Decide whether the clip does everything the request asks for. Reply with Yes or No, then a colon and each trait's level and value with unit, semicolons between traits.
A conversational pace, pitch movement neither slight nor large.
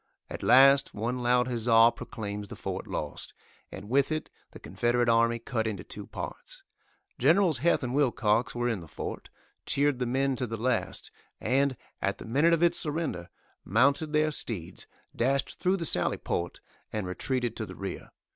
Yes: average, 175 wpm; average, 3.9 semitones